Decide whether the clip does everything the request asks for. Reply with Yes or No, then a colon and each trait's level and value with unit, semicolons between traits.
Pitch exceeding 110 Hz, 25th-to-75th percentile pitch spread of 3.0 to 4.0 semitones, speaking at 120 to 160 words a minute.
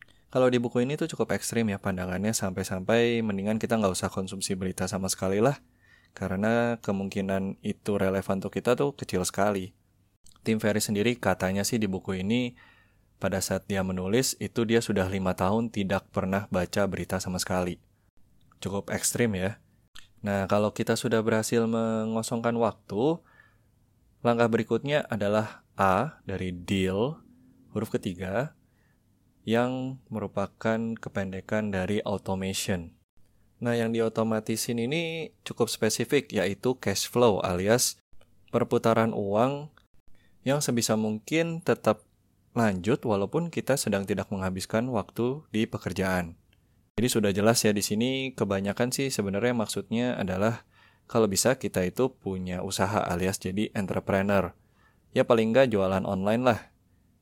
No: low, 105 Hz; average, 3.3 semitones; average, 130 wpm